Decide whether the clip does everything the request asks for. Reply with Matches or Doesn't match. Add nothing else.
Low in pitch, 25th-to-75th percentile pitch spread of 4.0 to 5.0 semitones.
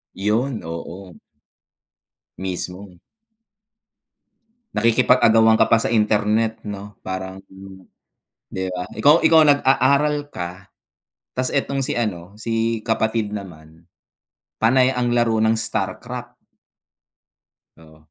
Matches